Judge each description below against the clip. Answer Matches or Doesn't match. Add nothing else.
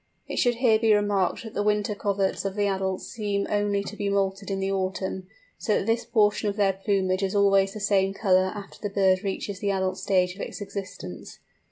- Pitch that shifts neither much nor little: Doesn't match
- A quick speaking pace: Matches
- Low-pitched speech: Doesn't match